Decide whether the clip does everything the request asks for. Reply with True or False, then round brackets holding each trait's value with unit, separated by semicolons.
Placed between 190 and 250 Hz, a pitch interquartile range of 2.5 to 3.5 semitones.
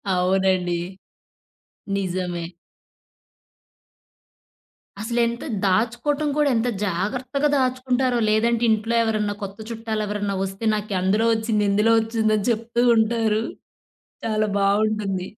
True (215 Hz; 2.9 semitones)